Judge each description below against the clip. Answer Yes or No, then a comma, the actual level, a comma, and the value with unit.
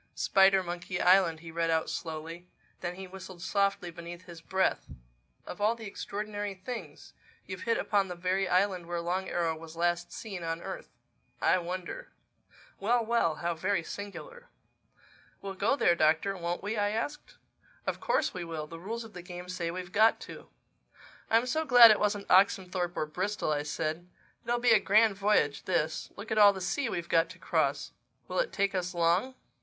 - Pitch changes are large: No, average, 3.2 semitones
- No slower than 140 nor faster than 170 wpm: No, average, 180 wpm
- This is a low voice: No, medium, 185 Hz